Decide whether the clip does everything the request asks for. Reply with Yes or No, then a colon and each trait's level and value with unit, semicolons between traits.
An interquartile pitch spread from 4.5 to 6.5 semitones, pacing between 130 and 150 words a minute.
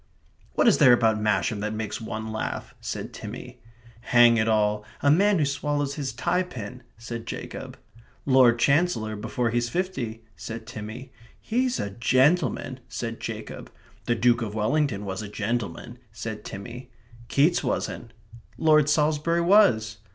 Yes: average, 5.2 semitones; average, 145 wpm